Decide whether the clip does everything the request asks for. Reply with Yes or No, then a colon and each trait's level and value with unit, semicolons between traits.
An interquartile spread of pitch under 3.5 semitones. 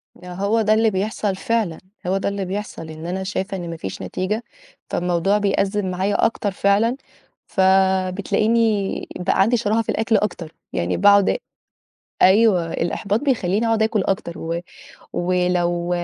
Yes: average, 2.9 semitones